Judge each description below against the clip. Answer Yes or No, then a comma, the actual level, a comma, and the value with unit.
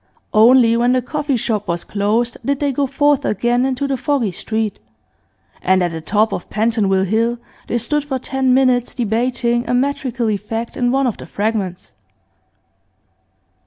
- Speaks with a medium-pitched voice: No, high, 235 Hz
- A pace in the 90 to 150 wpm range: No, average, 165 wpm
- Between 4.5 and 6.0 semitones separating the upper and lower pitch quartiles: No, average, 3.4 semitones